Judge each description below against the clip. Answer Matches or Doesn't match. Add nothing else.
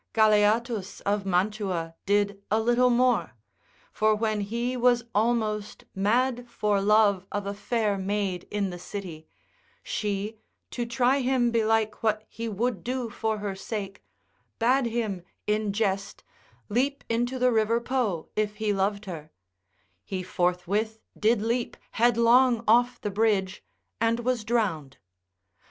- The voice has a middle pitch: Doesn't match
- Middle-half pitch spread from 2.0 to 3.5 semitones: Matches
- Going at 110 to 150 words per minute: Matches